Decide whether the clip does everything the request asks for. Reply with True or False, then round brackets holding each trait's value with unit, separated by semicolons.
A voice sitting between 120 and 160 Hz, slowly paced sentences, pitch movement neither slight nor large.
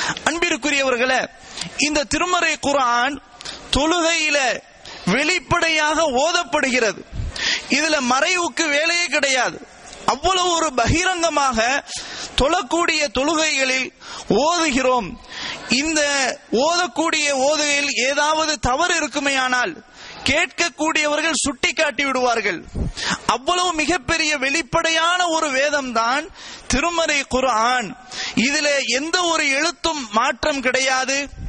False (300 Hz; 80 wpm; 3.9 semitones)